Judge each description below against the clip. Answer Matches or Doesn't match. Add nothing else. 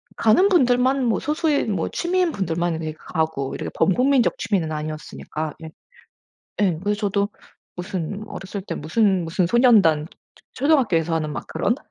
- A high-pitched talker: Matches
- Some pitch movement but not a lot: Doesn't match